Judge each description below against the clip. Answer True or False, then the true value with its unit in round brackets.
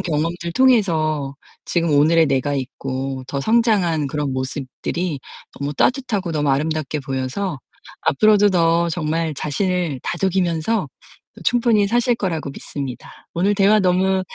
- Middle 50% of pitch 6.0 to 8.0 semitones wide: False (5.1 semitones)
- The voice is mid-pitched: True (165 Hz)